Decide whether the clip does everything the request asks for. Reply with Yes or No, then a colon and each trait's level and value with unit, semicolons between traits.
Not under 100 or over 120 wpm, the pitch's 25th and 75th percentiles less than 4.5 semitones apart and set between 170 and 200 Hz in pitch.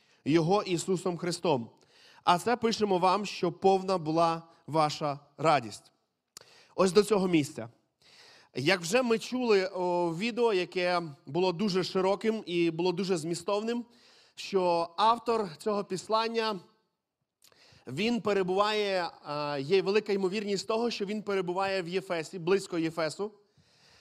Yes: average, 115 wpm; average, 3.5 semitones; high, 190 Hz